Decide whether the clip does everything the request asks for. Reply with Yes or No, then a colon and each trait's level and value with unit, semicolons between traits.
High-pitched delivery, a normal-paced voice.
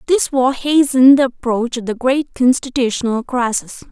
Yes: very high, 255 Hz; average, 155 wpm